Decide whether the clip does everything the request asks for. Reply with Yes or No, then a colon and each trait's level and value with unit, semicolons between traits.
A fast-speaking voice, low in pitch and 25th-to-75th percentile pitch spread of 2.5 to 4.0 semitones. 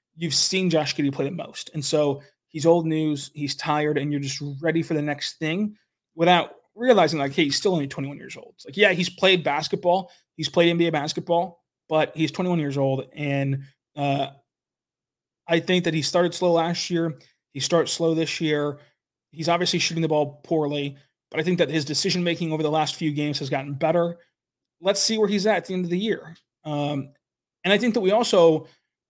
No: fast, 210 wpm; medium, 160 Hz; average, 3.2 semitones